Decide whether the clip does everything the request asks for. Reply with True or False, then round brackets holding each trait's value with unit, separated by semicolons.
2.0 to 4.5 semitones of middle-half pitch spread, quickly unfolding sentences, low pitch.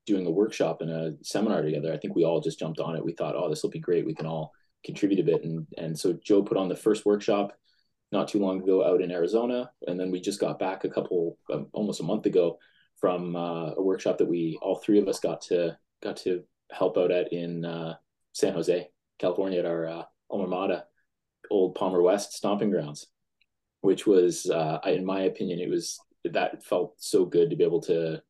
True (4.0 semitones; 225 wpm; 90 Hz)